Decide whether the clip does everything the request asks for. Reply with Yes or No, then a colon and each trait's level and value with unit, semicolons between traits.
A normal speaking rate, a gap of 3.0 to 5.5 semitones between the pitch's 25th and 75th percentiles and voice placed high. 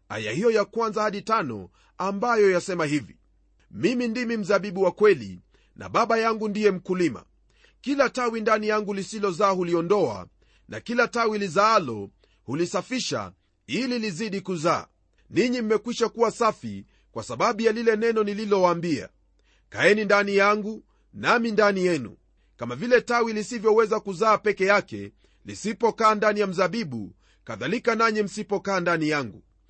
Yes: average, 130 wpm; average, 4.1 semitones; high, 210 Hz